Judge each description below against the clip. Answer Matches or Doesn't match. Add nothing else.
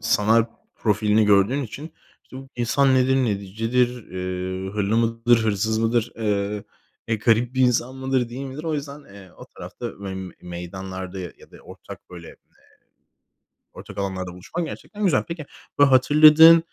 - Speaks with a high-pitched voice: Doesn't match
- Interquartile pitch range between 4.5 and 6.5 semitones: Matches